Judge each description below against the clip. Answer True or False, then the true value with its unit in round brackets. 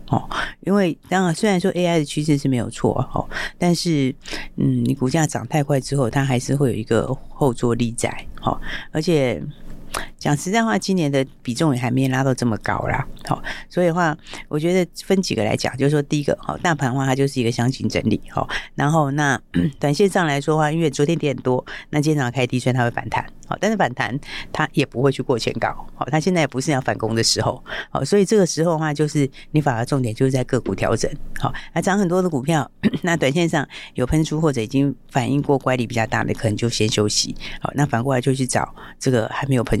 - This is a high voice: False (140 Hz)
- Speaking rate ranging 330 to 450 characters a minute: True (335 characters per minute)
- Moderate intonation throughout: True (4.2 semitones)